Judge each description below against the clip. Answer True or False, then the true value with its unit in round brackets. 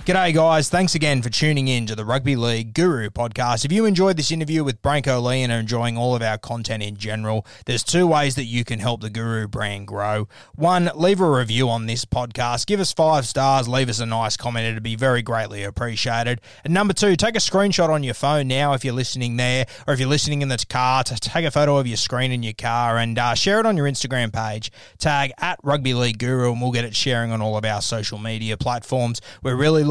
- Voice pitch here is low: True (125 Hz)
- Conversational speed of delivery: False (240 wpm)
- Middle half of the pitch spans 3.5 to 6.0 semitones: True (4.2 semitones)